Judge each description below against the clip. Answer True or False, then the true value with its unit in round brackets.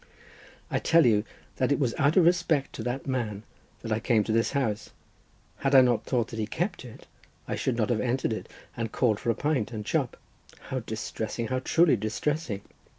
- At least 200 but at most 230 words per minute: True (205 wpm)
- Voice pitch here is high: False (120 Hz)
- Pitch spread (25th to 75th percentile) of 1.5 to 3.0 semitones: False (3.9 semitones)